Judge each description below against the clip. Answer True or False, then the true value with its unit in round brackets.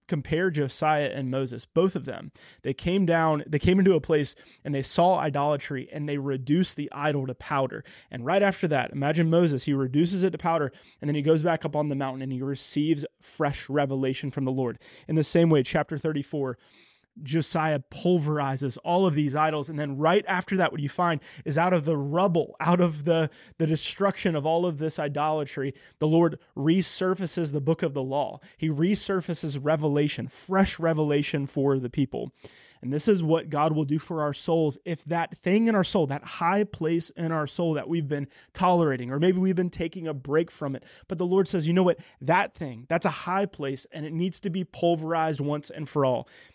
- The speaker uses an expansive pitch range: False (3.1 semitones)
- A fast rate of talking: True (210 wpm)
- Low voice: False (155 Hz)